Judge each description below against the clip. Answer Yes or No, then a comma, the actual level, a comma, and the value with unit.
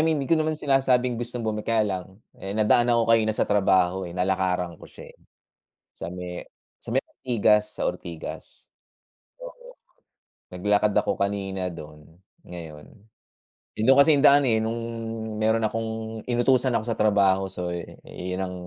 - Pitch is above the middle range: No, low, 105 Hz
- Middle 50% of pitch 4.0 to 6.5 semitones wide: Yes, average, 4.5 semitones